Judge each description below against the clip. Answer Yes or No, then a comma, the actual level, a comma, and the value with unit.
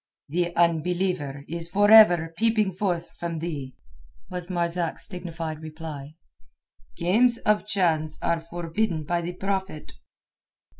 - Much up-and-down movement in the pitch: No, average, 2.7 semitones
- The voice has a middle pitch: Yes, medium, 170 Hz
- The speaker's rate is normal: No, slow, 115 wpm